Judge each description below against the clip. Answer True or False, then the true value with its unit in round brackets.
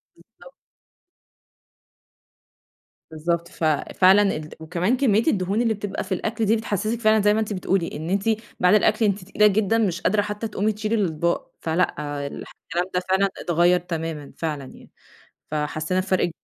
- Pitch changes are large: False (3.9 semitones)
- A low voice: False (190 Hz)